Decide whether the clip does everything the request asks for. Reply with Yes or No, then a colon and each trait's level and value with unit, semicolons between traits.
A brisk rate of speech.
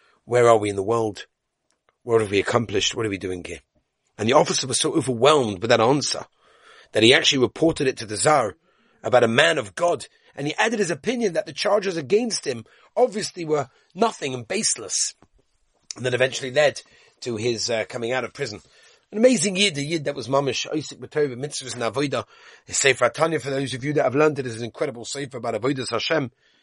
Yes: fast, 215 wpm